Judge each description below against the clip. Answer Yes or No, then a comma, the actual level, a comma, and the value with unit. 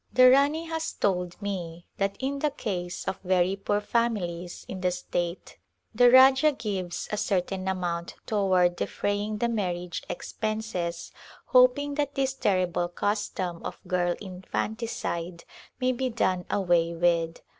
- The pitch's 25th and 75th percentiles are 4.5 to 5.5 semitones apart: Yes, average, 5.1 semitones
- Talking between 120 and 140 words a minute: Yes, slow, 135 wpm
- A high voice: Yes, high, 195 Hz